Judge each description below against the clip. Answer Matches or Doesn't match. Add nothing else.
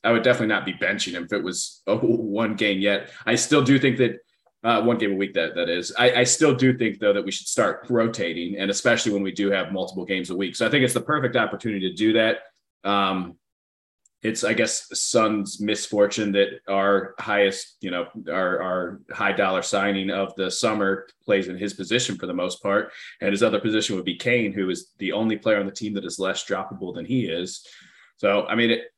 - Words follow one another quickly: Matches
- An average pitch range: Matches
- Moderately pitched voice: Doesn't match